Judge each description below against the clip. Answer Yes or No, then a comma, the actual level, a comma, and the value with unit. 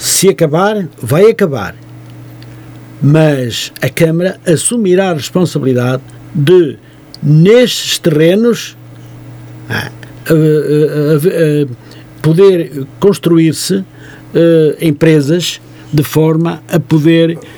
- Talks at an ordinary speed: No, slow, 70 wpm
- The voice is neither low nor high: Yes, medium, 155 Hz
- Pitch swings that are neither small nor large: Yes, average, 4.8 semitones